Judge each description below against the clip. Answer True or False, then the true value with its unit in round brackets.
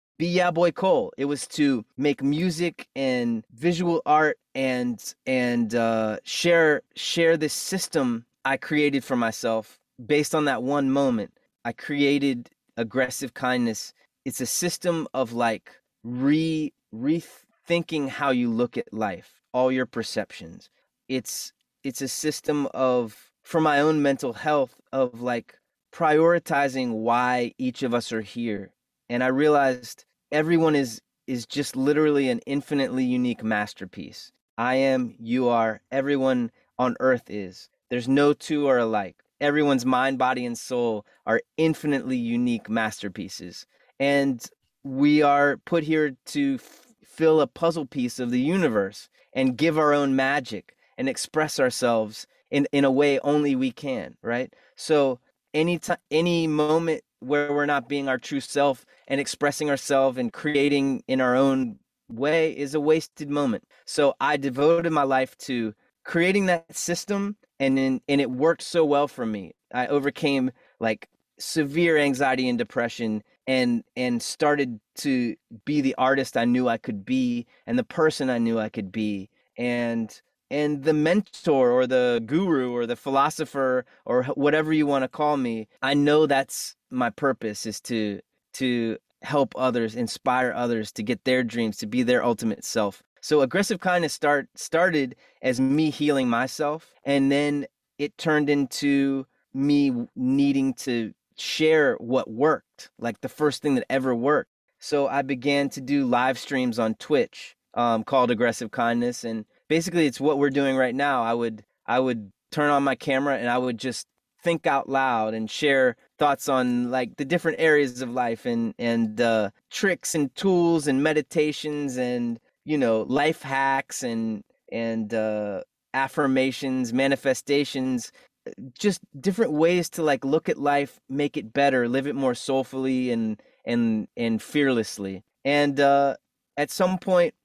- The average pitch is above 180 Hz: False (140 Hz)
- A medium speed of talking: True (155 wpm)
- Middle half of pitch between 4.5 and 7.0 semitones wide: False (3.8 semitones)